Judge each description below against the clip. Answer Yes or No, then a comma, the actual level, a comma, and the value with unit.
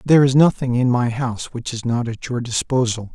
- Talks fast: Yes, fast, 230 wpm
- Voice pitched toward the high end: No, low, 125 Hz